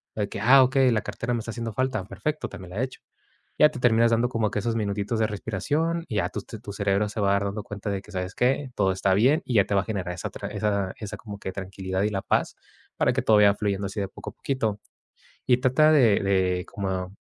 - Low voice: Yes, low, 105 Hz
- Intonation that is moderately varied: Yes, average, 3.2 semitones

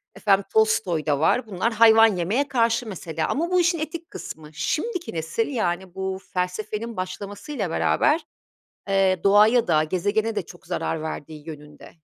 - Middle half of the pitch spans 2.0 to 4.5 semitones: No, average, 5.1 semitones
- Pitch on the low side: No, high, 200 Hz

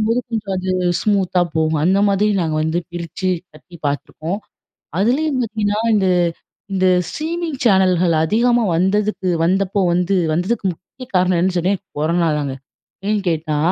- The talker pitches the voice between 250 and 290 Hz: No, high, 190 Hz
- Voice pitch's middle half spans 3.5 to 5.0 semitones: Yes, average, 3.8 semitones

